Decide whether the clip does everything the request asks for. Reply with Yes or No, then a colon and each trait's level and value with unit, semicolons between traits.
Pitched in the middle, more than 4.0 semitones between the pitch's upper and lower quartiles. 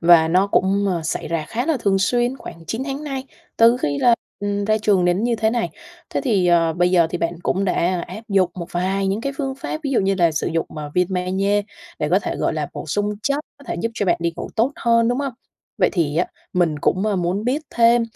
No: high, 195 Hz; average, 4.9 semitones